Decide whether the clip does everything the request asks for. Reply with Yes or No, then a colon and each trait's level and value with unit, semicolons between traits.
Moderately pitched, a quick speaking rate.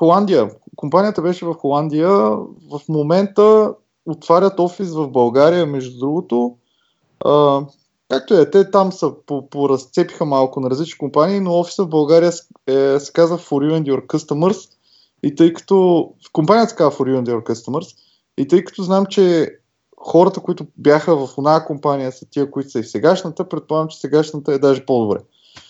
Yes: medium, 155 Hz; fast, 170 wpm